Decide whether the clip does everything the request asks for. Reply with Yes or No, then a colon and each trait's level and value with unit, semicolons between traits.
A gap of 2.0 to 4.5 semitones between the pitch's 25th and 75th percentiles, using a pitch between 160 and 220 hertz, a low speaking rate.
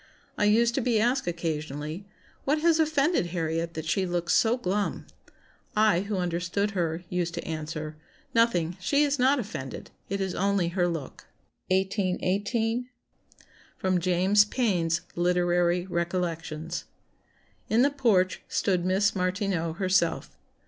Yes: average, 3.8 semitones; medium, 185 Hz; slow, 130 wpm